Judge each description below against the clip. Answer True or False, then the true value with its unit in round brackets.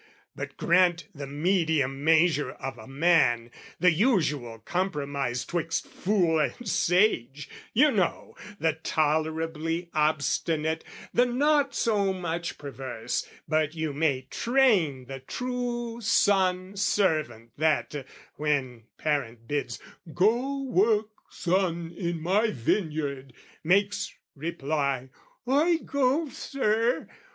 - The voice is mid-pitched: True (165 Hz)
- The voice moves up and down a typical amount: False (6.1 semitones)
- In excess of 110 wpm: False (105 wpm)